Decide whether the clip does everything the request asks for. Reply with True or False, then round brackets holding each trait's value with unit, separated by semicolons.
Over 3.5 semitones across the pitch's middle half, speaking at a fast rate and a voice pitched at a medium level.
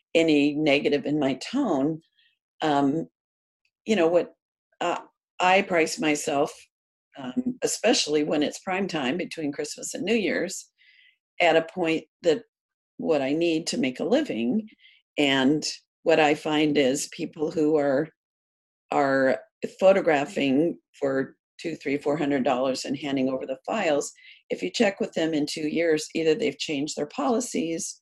False (4.7 semitones; 150 wpm; 155 Hz)